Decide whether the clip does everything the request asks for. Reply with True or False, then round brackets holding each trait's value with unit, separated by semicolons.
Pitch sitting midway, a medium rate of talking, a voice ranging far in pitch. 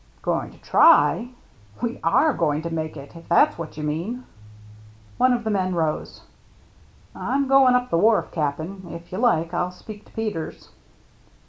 True (180 Hz; 180 wpm; 6.2 semitones)